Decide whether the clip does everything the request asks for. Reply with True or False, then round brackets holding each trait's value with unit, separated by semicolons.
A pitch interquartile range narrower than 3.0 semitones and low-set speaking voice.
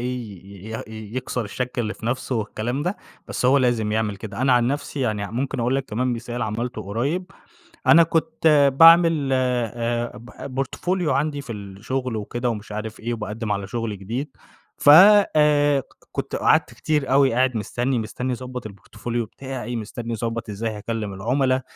False (3.5 semitones; 120 Hz)